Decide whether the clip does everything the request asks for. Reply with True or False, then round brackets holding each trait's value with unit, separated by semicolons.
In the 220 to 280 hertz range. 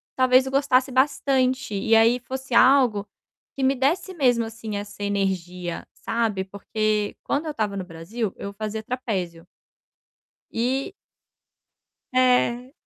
True (230 Hz)